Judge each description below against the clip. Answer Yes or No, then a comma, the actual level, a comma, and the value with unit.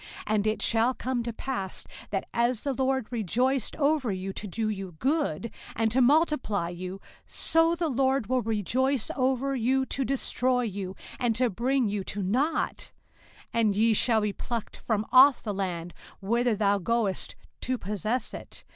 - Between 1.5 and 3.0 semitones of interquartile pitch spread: No, average, 4.2 semitones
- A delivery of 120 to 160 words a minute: No, average, 170 wpm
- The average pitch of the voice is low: No, high, 235 Hz